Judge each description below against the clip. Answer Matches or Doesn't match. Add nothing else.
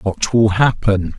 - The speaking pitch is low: Matches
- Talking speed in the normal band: Matches